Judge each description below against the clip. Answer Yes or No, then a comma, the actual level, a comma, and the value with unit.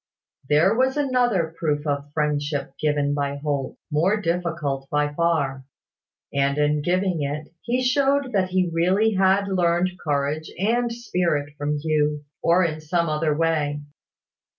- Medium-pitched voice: Yes, medium, 160 Hz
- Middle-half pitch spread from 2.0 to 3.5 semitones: No, average, 4.2 semitones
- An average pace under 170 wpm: Yes, average, 140 wpm